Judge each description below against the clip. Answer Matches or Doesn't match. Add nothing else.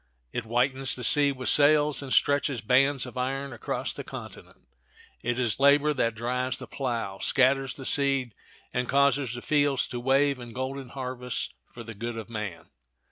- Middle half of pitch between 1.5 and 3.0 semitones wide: Matches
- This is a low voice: Matches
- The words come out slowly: Doesn't match